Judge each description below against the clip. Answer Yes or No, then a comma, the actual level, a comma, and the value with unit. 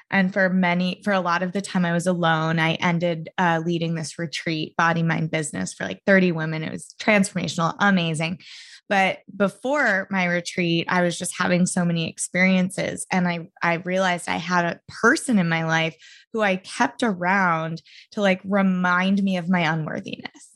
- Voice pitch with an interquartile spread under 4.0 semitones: Yes, average, 2.7 semitones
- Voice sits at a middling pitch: Yes, medium, 180 Hz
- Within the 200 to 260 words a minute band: No, average, 180 wpm